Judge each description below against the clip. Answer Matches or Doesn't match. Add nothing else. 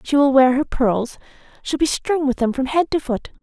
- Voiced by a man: Doesn't match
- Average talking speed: Doesn't match